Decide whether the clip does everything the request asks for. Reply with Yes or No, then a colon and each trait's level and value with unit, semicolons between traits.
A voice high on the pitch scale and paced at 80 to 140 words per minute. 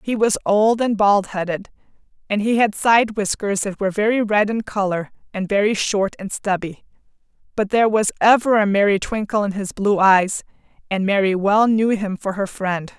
No: high, 205 Hz; average, 190 wpm